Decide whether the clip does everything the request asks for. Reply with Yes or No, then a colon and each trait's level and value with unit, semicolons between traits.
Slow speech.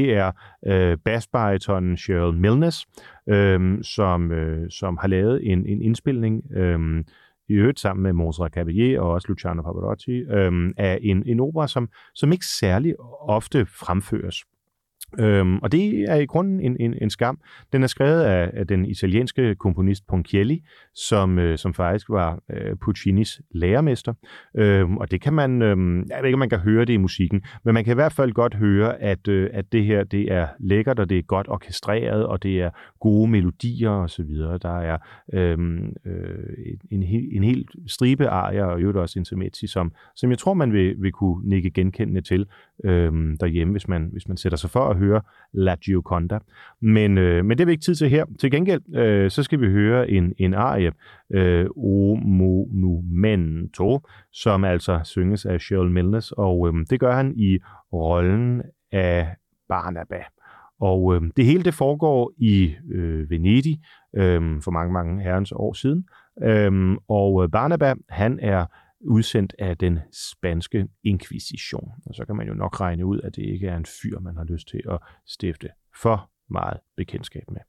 No: average, 180 wpm